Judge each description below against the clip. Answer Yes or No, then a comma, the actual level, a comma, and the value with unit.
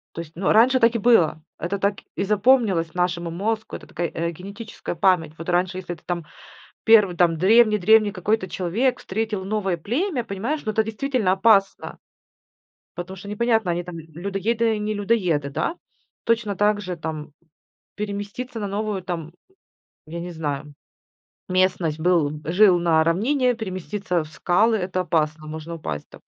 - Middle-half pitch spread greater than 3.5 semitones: Yes, average, 4.1 semitones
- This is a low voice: No, high, 190 Hz